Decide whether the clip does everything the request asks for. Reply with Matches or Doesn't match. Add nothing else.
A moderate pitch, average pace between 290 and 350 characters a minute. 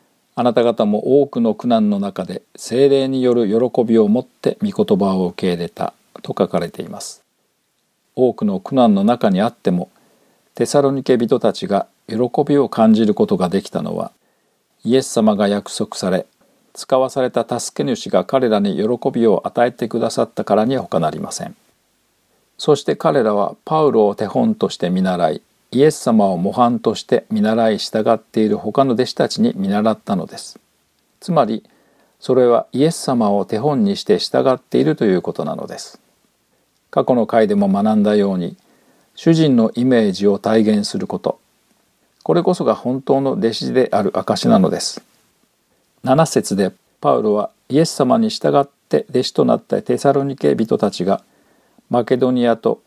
Doesn't match